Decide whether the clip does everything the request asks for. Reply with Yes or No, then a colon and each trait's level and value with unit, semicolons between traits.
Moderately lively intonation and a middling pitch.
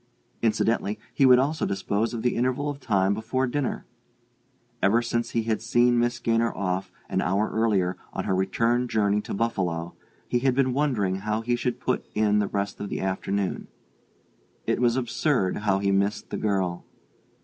No: average, 3.6 semitones; low, 110 Hz